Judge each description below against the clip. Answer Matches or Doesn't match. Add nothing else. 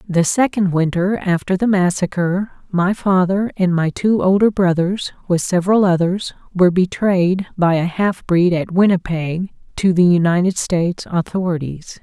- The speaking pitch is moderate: Matches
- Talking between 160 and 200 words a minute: Doesn't match